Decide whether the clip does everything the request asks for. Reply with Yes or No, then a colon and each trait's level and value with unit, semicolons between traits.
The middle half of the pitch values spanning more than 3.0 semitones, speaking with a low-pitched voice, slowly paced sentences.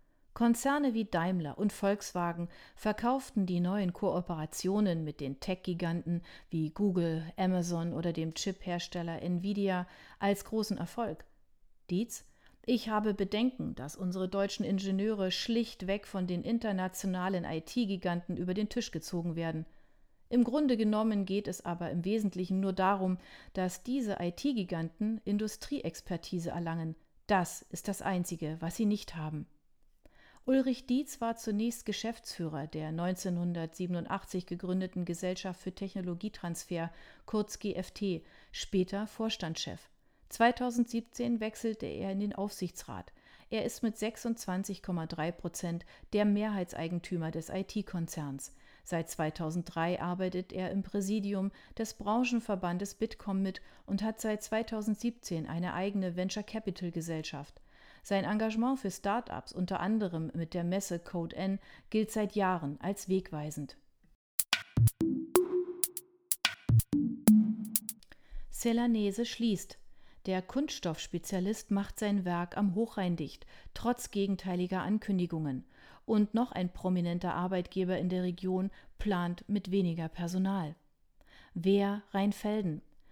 No: average, 3.6 semitones; high, 190 Hz; slow, 110 wpm